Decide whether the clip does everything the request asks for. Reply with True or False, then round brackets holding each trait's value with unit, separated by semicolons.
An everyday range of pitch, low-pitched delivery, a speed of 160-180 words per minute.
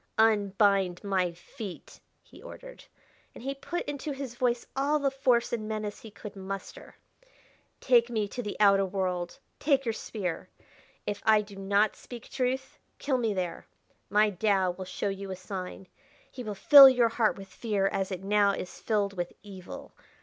False (3.8 semitones; 210 Hz; 170 wpm)